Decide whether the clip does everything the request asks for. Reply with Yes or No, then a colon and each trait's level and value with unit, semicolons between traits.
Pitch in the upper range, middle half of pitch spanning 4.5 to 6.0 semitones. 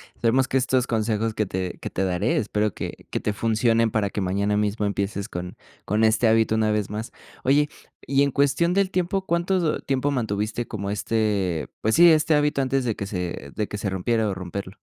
No: low, 110 Hz; average, 4.8 semitones